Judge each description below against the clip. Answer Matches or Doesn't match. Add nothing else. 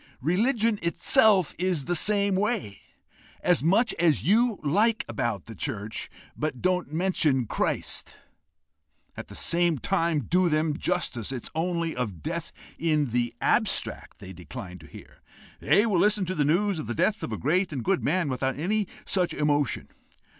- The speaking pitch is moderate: Matches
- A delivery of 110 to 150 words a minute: Doesn't match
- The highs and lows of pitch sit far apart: Matches